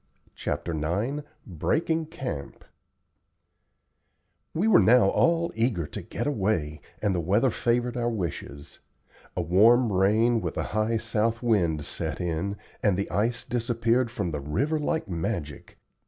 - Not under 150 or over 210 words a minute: No, average, 140 wpm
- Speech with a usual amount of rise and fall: No, wide, 5.8 semitones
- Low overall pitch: Yes, low, 110 Hz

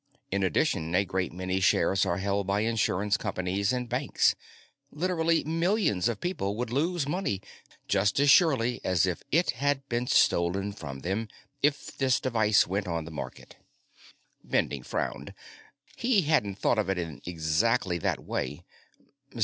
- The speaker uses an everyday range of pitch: No, wide, 6.8 semitones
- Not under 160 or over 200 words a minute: No, average, 150 wpm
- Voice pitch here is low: Yes, low, 105 Hz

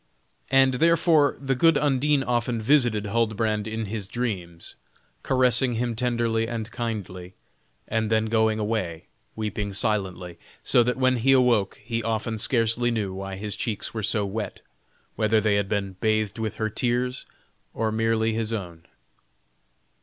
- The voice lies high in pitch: No, low, 110 Hz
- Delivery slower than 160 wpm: Yes, average, 150 wpm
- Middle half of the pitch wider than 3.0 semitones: No, average, 2.7 semitones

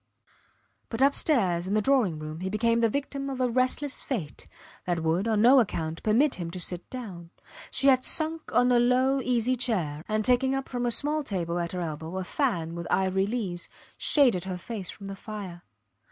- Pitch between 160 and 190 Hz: No, high, 215 Hz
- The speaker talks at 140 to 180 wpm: No, average, 195 wpm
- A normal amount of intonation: No, wide, 6.4 semitones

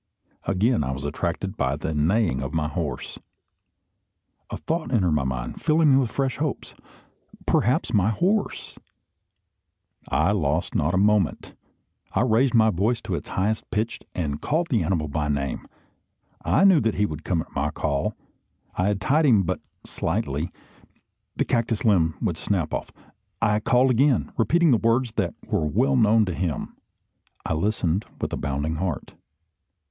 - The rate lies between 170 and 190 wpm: No, average, 160 wpm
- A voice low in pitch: Yes, low, 100 Hz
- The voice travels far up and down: Yes, wide, 7.3 semitones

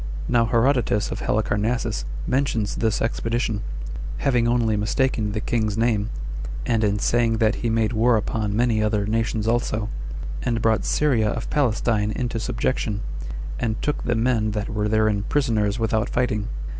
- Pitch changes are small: Yes, narrow, 2.0 semitones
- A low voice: Yes, low, 110 Hz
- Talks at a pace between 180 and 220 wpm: No, average, 150 wpm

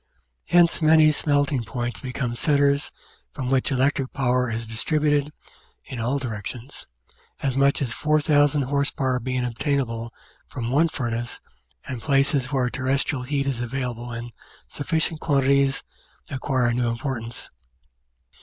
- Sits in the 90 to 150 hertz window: Yes, low, 135 Hz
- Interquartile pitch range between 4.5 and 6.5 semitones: No, average, 2.9 semitones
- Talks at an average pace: No, slow, 125 wpm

